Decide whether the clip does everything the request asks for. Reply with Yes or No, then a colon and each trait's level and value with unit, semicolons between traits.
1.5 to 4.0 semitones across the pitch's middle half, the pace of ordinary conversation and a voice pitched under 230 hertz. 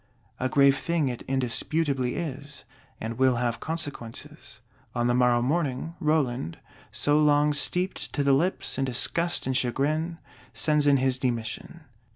Yes: average, 3.5 semitones; average, 145 wpm; medium, 140 Hz